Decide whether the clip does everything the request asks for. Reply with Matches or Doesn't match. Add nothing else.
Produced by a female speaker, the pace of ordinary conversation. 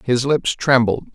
Doesn't match